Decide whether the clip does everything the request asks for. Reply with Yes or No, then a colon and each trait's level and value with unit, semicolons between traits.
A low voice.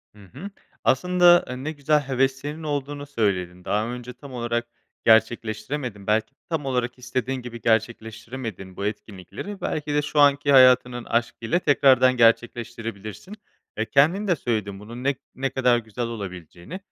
Yes: low, 125 Hz